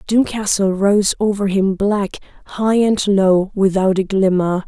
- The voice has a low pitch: No, high, 200 Hz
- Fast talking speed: No, average, 155 wpm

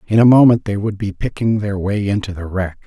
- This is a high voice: No, low, 100 Hz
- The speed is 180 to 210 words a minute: No, fast, 250 wpm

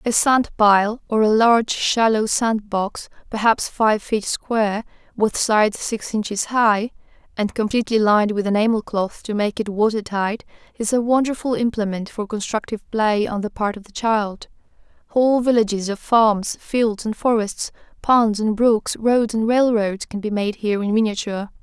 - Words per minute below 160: No, average, 165 wpm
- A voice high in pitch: Yes, high, 220 Hz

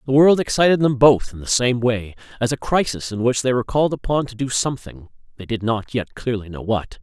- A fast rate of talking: Yes, fast, 230 wpm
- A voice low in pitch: Yes, low, 125 Hz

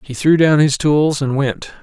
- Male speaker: Yes, male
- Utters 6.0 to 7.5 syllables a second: No, 4.3 syllables/s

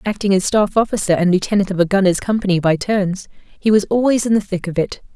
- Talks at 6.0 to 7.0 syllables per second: Yes, 6.3 syllables/s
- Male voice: No, female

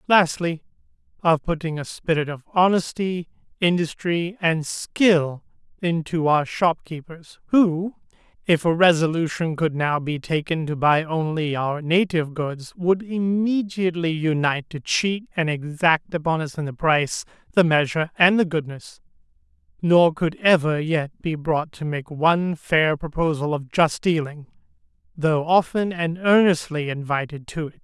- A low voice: No, medium, 165 Hz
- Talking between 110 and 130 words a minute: No, average, 140 wpm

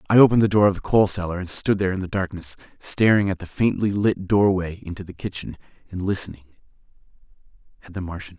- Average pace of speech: No, fast, 215 wpm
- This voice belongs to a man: Yes, male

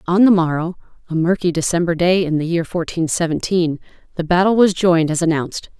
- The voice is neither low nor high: Yes, medium, 170 Hz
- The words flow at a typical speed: Yes, average, 185 wpm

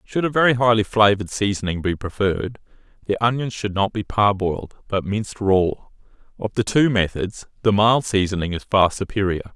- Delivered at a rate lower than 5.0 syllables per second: No, 5.6 syllables/s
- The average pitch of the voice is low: Yes, low, 105 Hz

